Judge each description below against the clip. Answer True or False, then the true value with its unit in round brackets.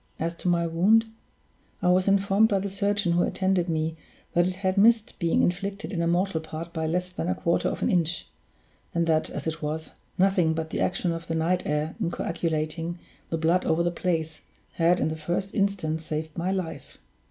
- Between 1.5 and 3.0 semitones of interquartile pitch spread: True (2.7 semitones)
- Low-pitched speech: False (170 Hz)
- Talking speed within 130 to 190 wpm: False (205 wpm)